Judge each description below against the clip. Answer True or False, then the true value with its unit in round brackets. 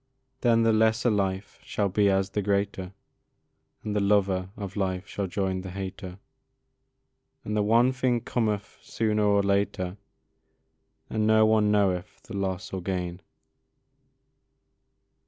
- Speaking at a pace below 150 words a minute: True (135 wpm)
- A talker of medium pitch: False (100 Hz)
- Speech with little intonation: True (2.3 semitones)